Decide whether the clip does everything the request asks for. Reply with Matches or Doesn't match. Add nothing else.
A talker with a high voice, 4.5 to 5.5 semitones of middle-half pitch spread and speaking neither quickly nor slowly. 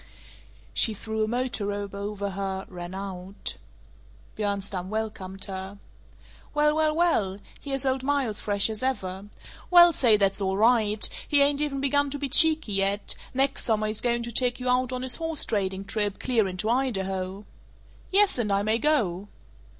Matches